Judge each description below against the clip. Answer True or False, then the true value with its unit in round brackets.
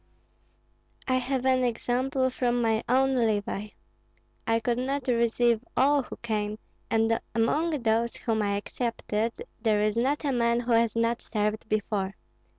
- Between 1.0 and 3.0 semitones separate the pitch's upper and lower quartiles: True (2.6 semitones)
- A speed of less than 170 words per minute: True (150 wpm)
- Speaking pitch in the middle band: False (235 Hz)